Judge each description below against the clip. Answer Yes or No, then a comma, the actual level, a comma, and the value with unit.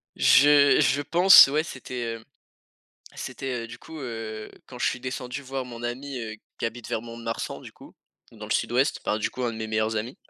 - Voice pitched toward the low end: Yes, low, 120 Hz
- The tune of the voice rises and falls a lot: No, average, 2.9 semitones